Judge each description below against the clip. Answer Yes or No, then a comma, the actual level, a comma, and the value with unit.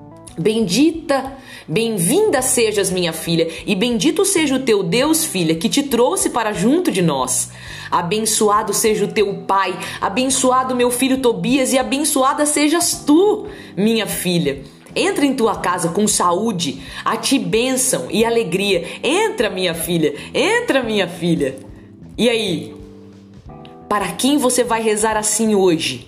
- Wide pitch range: Yes, wide, 6.9 semitones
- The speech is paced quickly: No, average, 140 wpm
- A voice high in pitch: Yes, high, 220 Hz